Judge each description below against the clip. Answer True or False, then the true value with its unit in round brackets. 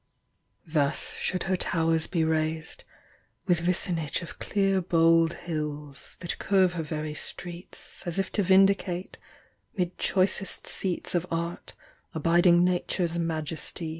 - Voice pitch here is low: False (170 Hz)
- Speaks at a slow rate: True (130 wpm)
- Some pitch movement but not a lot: False (2.2 semitones)